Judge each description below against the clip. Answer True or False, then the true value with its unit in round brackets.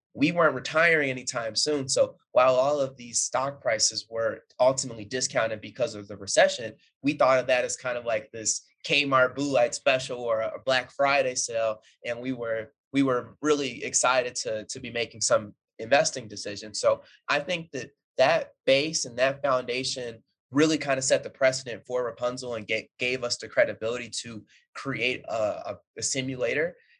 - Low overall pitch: True (125 Hz)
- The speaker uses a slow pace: False (180 wpm)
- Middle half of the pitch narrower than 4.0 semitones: True (3.1 semitones)